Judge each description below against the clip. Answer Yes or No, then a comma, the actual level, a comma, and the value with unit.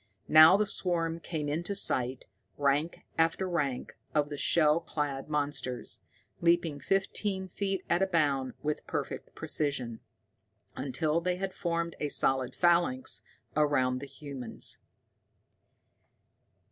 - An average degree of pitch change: Yes, average, 3.7 semitones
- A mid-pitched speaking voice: Yes, medium, 150 Hz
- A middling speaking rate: No, slow, 120 wpm